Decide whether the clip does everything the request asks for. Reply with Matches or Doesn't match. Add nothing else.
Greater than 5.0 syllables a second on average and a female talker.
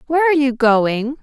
Matches